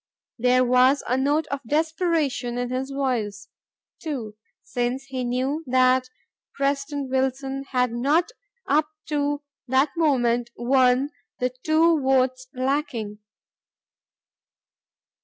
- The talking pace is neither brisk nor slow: No, slow, 105 wpm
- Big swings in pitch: No, narrow, 2.4 semitones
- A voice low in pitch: No, very high, 265 Hz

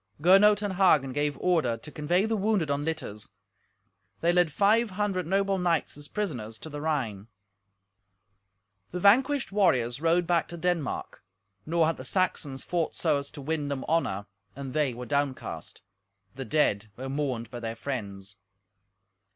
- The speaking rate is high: No, average, 160 wpm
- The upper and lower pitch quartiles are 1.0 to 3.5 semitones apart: No, average, 5.3 semitones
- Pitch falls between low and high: Yes, medium, 155 Hz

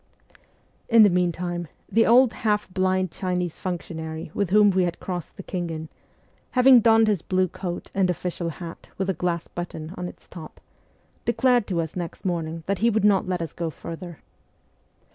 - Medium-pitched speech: Yes, medium, 180 Hz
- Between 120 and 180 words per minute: Yes, average, 175 wpm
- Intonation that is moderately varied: Yes, average, 3.1 semitones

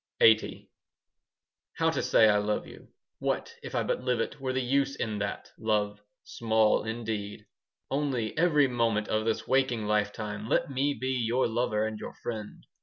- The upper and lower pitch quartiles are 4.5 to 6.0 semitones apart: No, average, 3.3 semitones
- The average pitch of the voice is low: Yes, low, 115 Hz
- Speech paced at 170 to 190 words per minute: Yes, average, 175 wpm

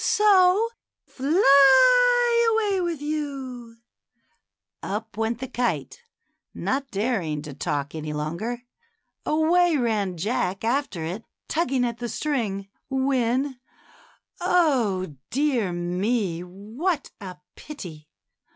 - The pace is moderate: No, slow, 105 wpm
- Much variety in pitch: Yes, wide, 7.7 semitones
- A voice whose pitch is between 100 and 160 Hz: No, high, 245 Hz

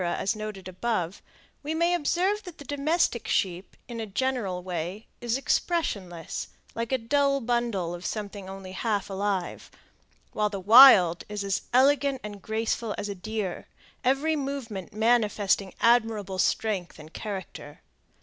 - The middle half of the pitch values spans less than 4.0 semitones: No, average, 5.3 semitones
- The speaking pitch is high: Yes, high, 215 Hz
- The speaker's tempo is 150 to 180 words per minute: No, average, 140 wpm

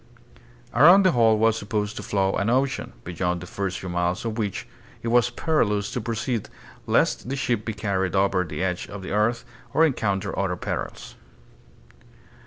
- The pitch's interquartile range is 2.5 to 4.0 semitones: Yes, average, 3.5 semitones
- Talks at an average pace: Yes, average, 175 wpm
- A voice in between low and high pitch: No, low, 105 Hz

